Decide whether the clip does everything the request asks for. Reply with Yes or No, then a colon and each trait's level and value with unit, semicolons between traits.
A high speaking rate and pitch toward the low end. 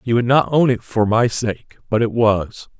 Yes: fast, 235 wpm; low, 115 Hz